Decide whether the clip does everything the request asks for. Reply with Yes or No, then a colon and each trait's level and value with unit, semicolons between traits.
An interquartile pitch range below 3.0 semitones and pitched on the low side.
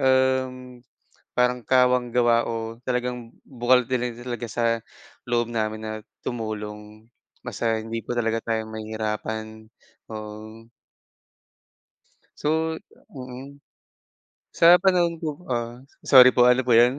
Yes: narrow, 2.4 semitones; low, 120 Hz